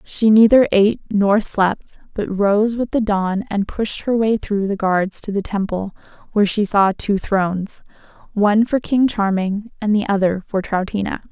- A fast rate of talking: No, average, 180 wpm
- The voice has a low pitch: No, high, 205 Hz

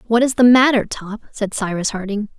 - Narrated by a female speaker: Yes, female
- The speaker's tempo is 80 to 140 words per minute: No, average, 200 wpm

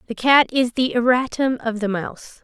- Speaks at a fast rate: No, average, 195 wpm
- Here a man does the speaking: No, female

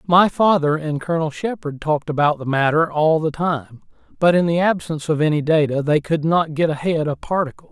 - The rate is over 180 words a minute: Yes, average, 200 wpm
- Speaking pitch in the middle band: Yes, medium, 155 Hz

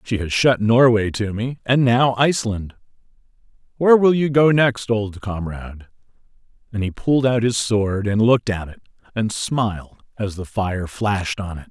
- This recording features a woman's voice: No, male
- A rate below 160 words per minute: No, average, 175 wpm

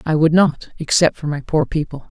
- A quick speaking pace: No, average, 190 wpm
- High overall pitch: No, medium, 155 Hz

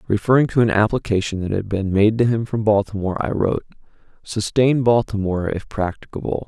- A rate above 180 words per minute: No, average, 165 wpm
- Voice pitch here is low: Yes, low, 105 Hz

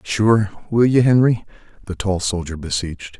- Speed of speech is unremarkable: No, slow, 130 wpm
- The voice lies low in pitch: Yes, low, 100 Hz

